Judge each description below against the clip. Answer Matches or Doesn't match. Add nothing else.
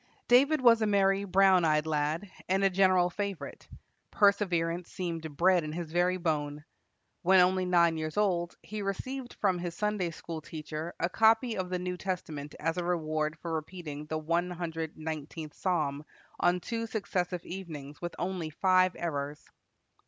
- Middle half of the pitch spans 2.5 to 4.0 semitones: Matches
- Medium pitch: Matches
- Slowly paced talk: Doesn't match